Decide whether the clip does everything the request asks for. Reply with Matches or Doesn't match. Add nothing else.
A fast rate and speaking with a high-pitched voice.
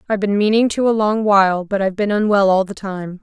Matches